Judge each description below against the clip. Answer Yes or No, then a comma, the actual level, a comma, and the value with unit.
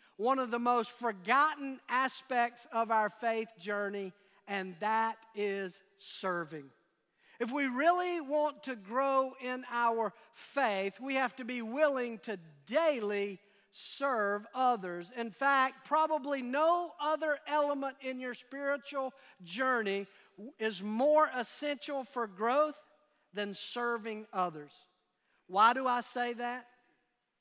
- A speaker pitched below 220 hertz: No, high, 245 Hz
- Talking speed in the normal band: No, slow, 120 wpm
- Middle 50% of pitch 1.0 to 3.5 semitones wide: No, average, 4.9 semitones